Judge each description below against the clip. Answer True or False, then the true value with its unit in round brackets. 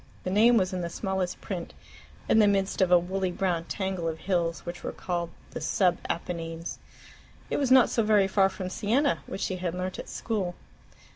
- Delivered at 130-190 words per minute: False (200 wpm)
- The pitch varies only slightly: True (2.3 semitones)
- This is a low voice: False (185 Hz)